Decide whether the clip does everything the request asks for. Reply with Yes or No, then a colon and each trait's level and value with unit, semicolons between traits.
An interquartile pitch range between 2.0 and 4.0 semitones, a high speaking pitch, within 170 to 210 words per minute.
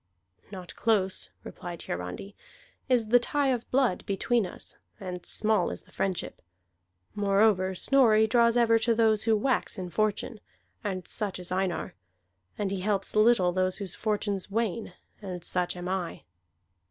No: average, 3.4 semitones; high, 205 Hz; average, 150 wpm